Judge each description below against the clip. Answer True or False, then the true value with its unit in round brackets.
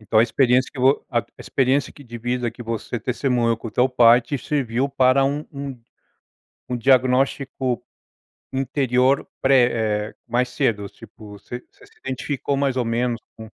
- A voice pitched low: True (125 Hz)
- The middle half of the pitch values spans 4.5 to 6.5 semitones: False (2.4 semitones)